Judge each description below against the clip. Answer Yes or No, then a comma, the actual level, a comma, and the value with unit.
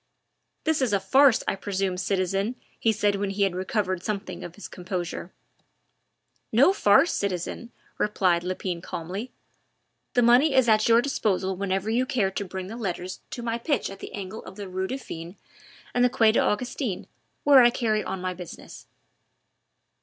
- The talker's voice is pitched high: Yes, high, 200 Hz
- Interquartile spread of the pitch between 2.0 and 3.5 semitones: No, average, 4.1 semitones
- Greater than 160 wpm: Yes, average, 170 wpm